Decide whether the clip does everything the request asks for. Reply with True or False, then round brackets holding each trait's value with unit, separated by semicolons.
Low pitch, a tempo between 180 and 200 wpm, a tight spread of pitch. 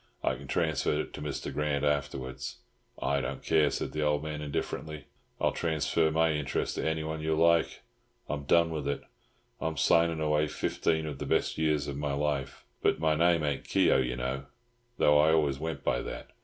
True (75 Hz; 190 wpm; 1.9 semitones)